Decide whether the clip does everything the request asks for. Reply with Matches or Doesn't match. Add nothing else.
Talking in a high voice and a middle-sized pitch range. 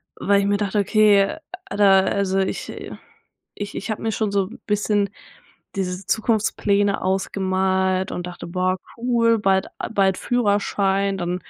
Doesn't match